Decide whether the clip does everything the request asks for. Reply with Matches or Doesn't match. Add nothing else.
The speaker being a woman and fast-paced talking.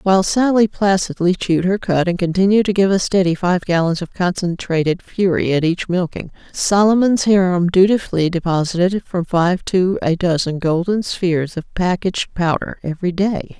Doesn't match